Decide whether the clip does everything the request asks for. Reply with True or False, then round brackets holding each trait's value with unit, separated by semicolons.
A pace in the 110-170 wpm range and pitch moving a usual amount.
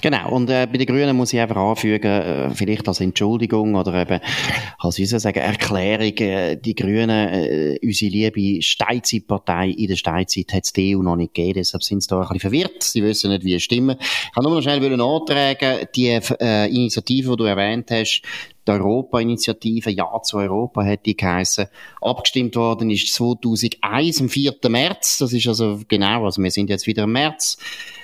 False (190 wpm; 3.7 semitones)